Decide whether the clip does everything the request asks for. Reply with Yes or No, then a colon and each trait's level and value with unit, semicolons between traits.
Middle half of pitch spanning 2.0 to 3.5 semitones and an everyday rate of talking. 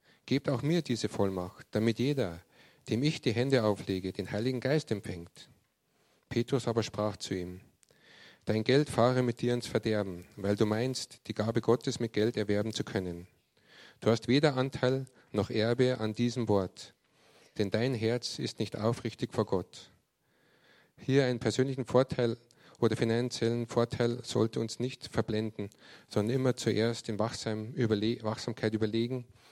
Yes: average, 2.9 semitones; average, 150 wpm